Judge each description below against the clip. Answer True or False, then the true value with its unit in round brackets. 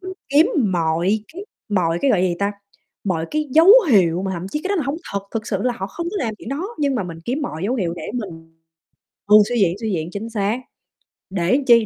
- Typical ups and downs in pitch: False (7.0 semitones)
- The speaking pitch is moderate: False (210 Hz)